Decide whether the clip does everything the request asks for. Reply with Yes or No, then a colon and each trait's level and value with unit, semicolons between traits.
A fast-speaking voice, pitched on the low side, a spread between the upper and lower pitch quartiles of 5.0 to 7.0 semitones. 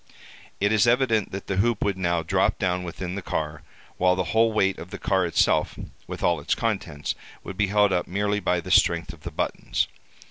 No: fast, 210 wpm; very low, 95 Hz; average, 3.0 semitones